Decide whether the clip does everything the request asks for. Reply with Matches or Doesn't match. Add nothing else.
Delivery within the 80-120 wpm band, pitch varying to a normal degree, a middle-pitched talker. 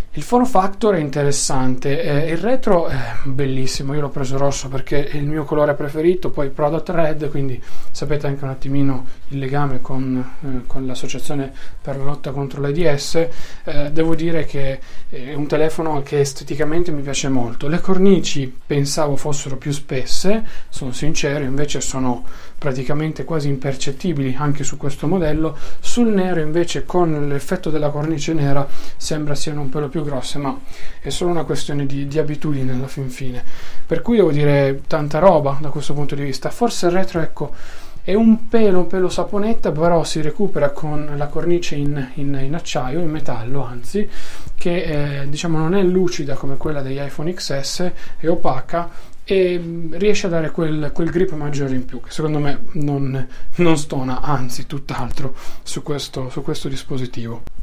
Doesn't match